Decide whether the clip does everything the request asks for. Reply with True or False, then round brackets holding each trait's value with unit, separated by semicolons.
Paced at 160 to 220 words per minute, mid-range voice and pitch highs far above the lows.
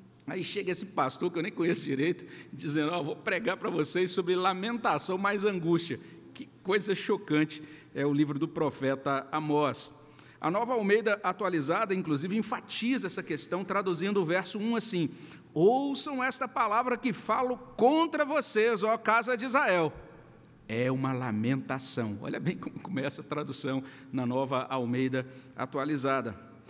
False (150 wpm; 175 Hz; 7.0 semitones)